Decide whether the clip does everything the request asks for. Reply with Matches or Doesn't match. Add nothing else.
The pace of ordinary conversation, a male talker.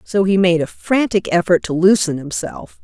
Doesn't match